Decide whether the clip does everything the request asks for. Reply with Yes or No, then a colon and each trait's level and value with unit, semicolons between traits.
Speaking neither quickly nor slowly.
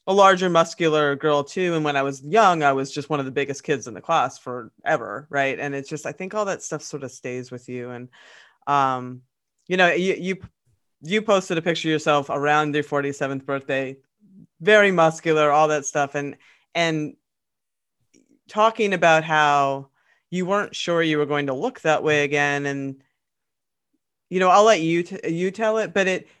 Yes: average, 195 wpm